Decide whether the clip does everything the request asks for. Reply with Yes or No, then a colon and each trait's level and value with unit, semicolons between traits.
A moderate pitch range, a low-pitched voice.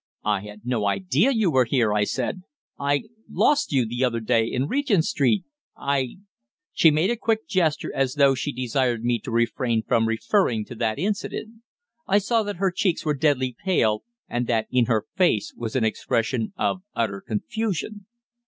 No: wide, 8.5 semitones; low, 130 Hz